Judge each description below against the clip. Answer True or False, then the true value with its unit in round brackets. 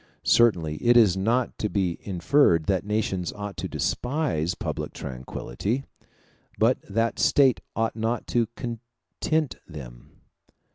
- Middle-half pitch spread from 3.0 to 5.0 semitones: False (5.4 semitones)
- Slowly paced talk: True (125 wpm)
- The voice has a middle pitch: False (105 Hz)